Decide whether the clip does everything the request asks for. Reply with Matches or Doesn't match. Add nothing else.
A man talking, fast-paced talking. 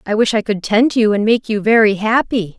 Doesn't match